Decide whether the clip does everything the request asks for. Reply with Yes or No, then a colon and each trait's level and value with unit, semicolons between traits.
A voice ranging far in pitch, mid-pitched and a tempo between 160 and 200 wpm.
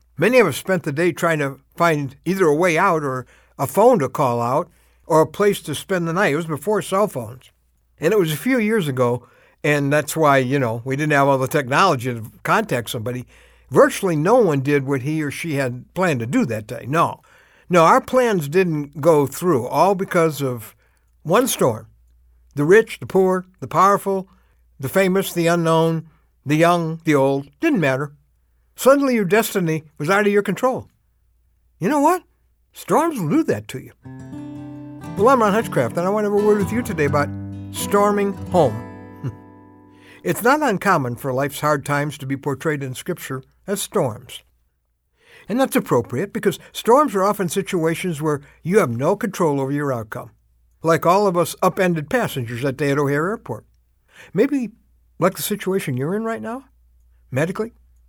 Yes: wide, 6.7 semitones; medium, 155 Hz; average, 185 wpm